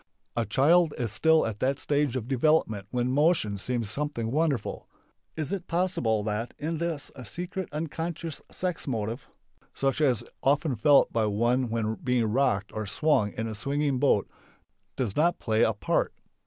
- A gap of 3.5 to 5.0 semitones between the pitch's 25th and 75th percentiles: No, wide, 5.5 semitones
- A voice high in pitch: No, low, 130 Hz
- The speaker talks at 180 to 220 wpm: No, average, 170 wpm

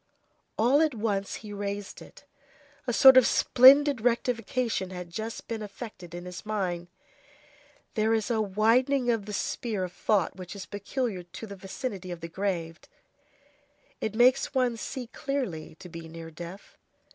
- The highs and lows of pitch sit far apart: No, average, 5.0 semitones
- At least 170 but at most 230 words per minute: No, average, 155 wpm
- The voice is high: Yes, high, 210 Hz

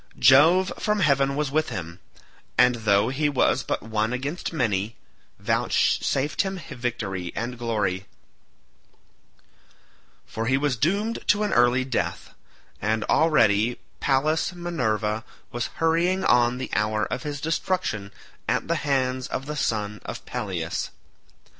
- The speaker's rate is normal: No, slow, 130 wpm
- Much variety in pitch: Yes, wide, 5.8 semitones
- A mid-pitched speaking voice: No, low, 130 Hz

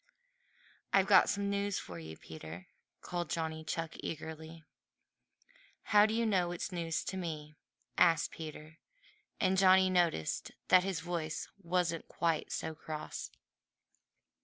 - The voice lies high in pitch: No, medium, 170 Hz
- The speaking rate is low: Yes, slow, 130 wpm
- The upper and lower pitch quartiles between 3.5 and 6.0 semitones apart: No, average, 3.0 semitones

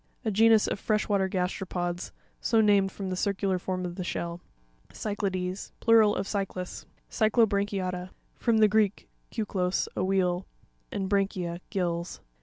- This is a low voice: No, high, 195 Hz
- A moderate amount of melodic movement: No, narrow, 2.3 semitones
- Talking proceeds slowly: Yes, slow, 130 wpm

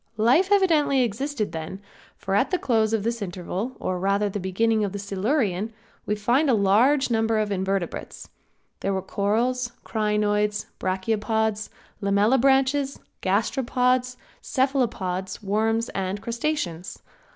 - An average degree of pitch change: Yes, average, 4.2 semitones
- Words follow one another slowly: Yes, slow, 130 wpm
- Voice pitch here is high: Yes, high, 215 Hz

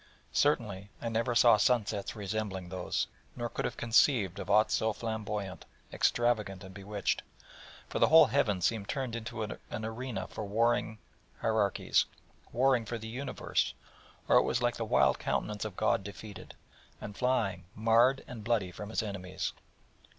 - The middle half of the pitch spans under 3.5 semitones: Yes, average, 2.8 semitones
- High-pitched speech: No, low, 110 Hz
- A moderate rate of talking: Yes, average, 160 wpm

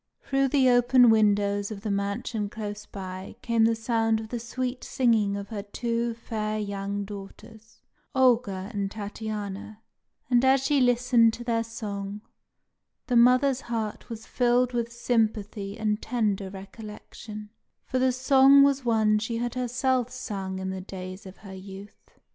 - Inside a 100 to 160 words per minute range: Yes, average, 155 wpm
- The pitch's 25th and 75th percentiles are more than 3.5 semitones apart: No, average, 3.2 semitones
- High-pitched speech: Yes, high, 225 Hz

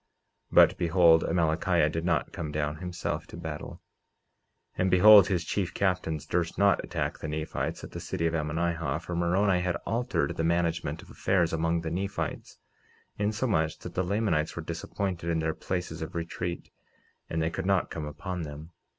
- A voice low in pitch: Yes, very low, 85 Hz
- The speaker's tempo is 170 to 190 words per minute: Yes, average, 175 wpm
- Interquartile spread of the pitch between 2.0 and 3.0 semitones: Yes, narrow, 2.5 semitones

